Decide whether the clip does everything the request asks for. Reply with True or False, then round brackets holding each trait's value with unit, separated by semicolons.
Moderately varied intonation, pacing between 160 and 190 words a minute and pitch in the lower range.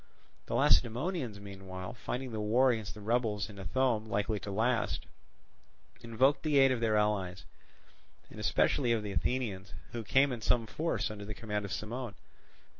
True (3.5 semitones; 165 wpm; 110 Hz)